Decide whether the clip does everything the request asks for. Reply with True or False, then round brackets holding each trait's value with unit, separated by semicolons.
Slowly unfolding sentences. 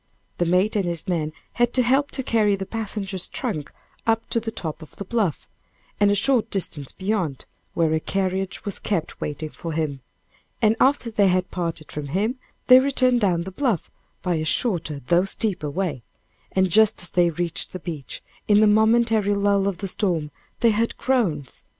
False (185 wpm)